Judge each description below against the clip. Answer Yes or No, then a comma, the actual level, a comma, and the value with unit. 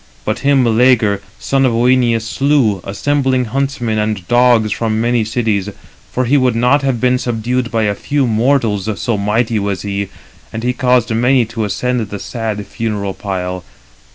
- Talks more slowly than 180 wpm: Yes, average, 165 wpm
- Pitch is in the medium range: No, low, 115 Hz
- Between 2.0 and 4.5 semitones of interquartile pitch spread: Yes, average, 3.1 semitones